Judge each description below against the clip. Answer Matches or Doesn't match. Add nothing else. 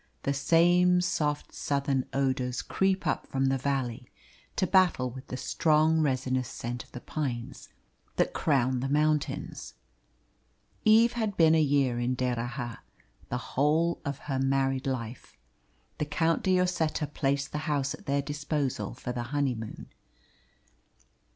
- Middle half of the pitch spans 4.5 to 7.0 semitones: Doesn't match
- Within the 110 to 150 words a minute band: Matches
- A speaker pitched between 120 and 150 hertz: Matches